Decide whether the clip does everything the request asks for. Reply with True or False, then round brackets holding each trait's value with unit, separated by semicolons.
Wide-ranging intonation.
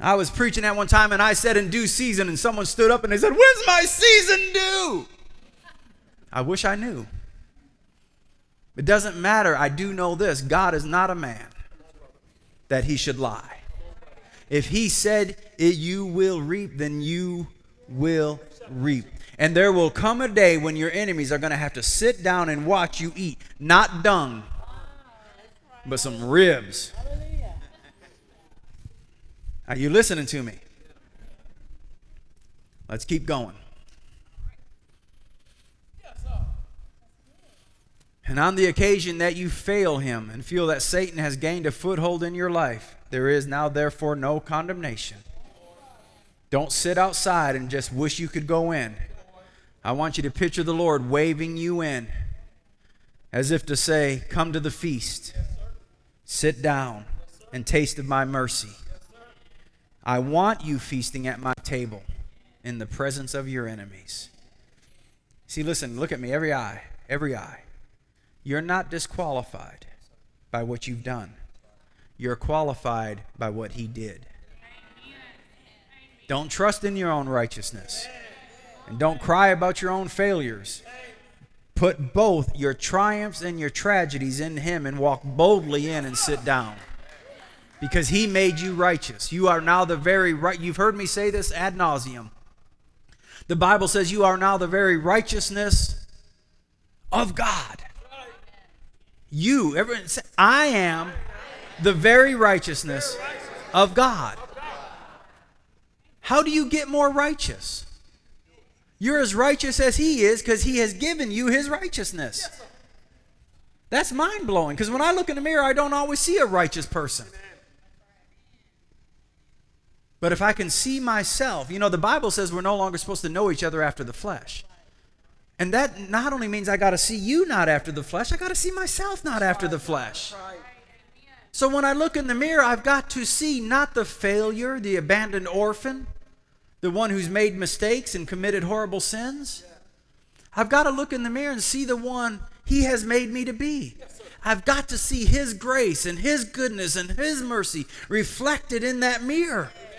True (7.8 semitones)